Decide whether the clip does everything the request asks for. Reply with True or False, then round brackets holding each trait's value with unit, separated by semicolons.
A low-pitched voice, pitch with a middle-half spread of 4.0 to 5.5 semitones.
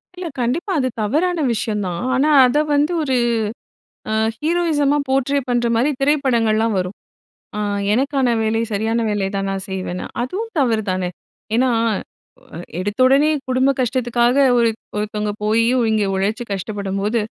False (235 Hz; 4.7 semitones)